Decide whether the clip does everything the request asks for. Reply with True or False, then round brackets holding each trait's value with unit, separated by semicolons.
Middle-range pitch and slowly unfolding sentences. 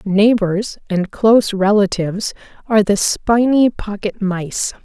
False (205 Hz; 110 wpm)